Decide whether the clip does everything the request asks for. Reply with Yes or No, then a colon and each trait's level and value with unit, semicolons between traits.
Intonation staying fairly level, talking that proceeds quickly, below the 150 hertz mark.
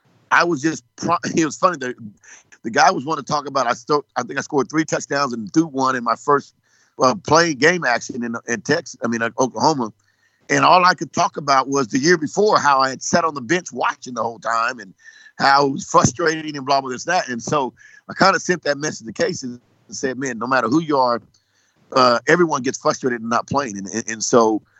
No: average, 5.1 semitones; fast, 235 wpm; medium, 140 Hz